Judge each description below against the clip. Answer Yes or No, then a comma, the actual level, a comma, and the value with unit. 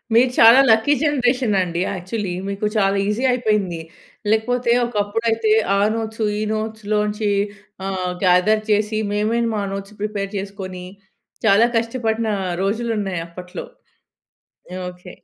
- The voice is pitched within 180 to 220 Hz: Yes, high, 210 Hz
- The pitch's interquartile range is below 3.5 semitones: Yes, narrow, 2.4 semitones